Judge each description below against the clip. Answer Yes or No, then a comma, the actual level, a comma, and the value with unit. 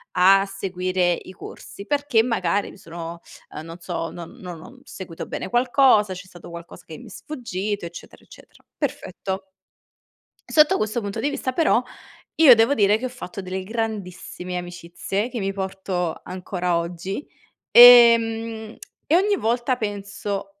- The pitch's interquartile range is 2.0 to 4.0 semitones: No, average, 4.5 semitones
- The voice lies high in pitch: Yes, high, 195 Hz